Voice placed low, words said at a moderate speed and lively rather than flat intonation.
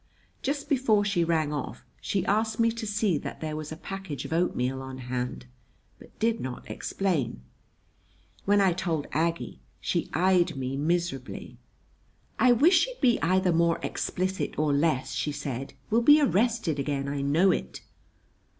No: medium, 170 Hz; average, 160 wpm; wide, 6.5 semitones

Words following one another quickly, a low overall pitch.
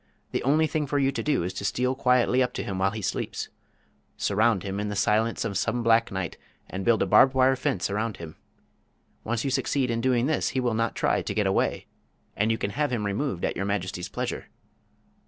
Yes: fast, 225 wpm; low, 115 Hz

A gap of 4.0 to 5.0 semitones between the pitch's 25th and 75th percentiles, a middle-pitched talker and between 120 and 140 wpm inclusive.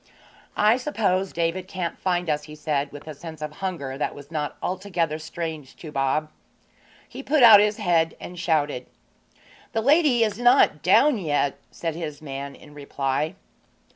No: average, 4.7 semitones; medium, 165 Hz; average, 165 wpm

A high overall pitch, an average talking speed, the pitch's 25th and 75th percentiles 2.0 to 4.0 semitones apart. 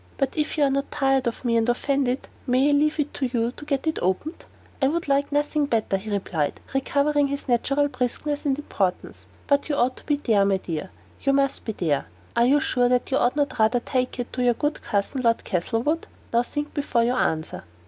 No: very high, 265 Hz; fast, 225 wpm; average, 3.7 semitones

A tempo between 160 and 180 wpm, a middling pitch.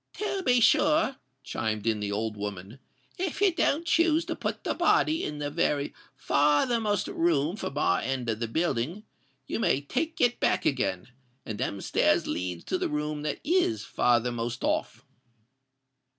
Yes: average, 165 wpm; medium, 150 Hz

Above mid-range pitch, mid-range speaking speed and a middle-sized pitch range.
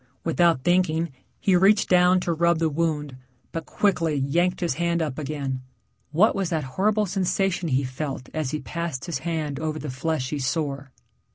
No: medium, 160 Hz; average, 170 wpm; average, 3.6 semitones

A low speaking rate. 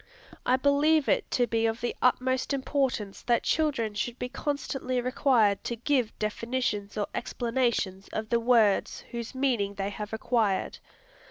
No: average, 150 wpm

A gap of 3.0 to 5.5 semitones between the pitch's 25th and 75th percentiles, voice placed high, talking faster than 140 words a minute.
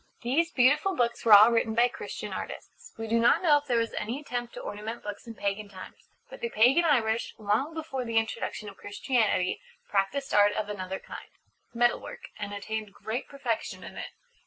Yes: average, 3.3 semitones; high, 230 Hz; average, 195 wpm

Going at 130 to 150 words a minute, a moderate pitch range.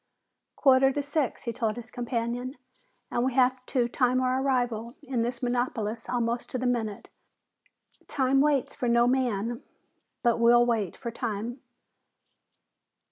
No: average, 140 wpm; narrow, 1.6 semitones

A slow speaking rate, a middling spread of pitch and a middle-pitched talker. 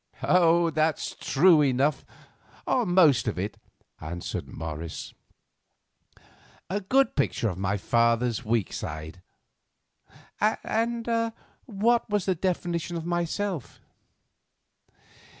No: slow, 95 wpm; wide, 8.6 semitones; medium, 160 Hz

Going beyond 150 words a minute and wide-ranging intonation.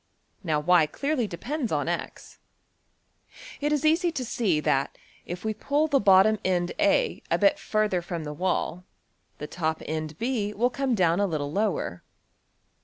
No: average, 145 wpm; wide, 7.9 semitones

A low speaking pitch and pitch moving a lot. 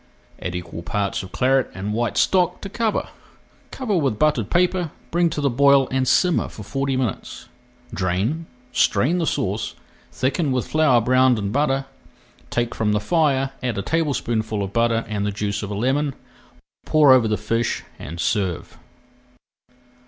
Yes: low, 125 Hz; wide, 5.7 semitones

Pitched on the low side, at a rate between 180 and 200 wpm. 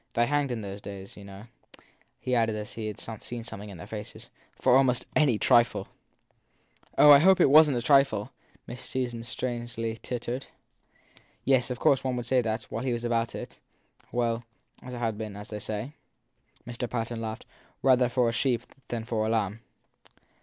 Yes: low, 120 Hz; average, 190 wpm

